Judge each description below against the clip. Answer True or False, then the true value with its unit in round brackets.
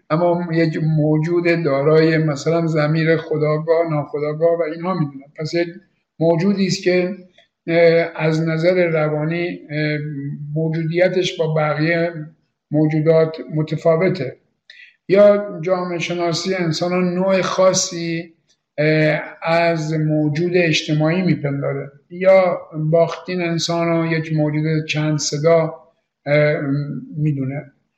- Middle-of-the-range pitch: True (165 Hz)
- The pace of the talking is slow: True (90 wpm)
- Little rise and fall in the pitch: True (2.1 semitones)